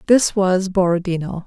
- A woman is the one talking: Yes, female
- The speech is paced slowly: Yes, slow, 125 wpm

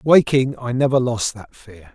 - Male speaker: Yes, male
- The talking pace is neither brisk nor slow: Yes, average, 185 wpm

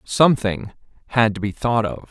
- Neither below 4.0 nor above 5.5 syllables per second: Yes, 5.1 syllables/s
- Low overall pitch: Yes, low, 110 Hz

